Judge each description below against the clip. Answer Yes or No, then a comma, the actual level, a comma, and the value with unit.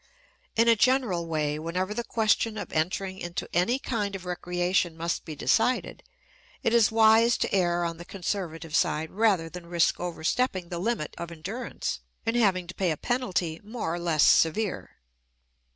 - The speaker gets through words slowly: No, average, 170 wpm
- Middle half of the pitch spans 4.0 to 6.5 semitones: Yes, average, 4.7 semitones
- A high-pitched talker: No, medium, 180 Hz